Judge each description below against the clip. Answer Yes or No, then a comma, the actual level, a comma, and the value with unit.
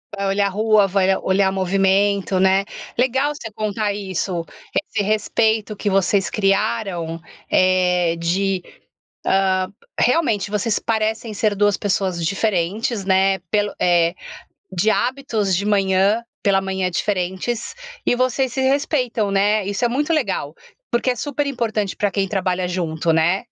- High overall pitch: Yes, high, 200 Hz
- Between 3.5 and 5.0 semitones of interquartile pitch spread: No, average, 2.7 semitones